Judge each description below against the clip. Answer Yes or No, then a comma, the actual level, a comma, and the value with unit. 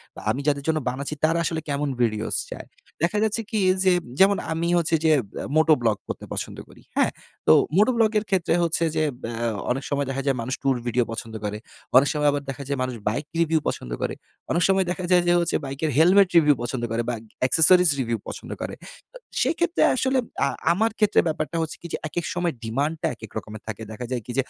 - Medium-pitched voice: Yes, medium, 155 Hz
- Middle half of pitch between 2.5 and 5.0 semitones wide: No, wide, 5.4 semitones